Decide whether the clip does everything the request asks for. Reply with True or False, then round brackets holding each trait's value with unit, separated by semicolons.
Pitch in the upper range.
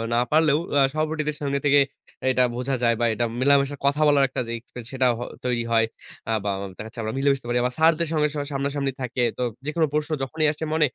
False (140 Hz)